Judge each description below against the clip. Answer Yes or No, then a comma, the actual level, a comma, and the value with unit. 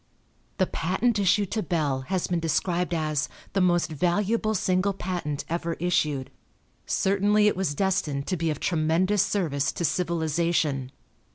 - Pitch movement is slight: No, average, 3.6 semitones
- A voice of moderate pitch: Yes, medium, 175 Hz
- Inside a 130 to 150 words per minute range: Yes, average, 145 wpm